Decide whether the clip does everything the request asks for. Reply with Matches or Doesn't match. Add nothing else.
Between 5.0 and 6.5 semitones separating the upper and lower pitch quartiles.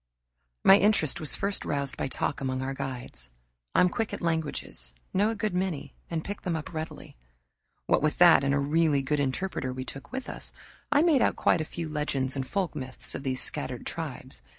Matches